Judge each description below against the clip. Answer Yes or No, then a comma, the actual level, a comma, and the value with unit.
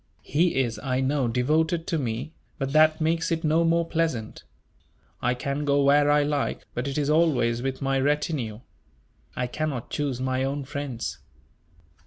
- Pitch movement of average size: Yes, average, 3.2 semitones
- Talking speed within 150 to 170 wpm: Yes, average, 165 wpm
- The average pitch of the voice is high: No, medium, 140 Hz